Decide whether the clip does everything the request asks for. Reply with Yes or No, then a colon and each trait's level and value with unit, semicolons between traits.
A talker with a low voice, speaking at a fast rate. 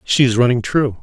Yes: low, 125 Hz; fast, 235 wpm